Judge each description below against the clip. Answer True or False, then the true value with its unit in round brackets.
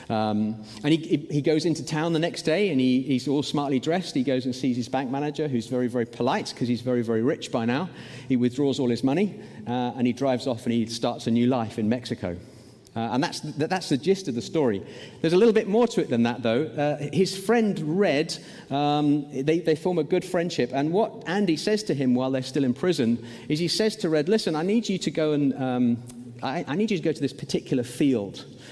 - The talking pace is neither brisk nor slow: False (245 wpm)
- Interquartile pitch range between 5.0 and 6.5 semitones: True (5.3 semitones)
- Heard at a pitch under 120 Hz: False (140 Hz)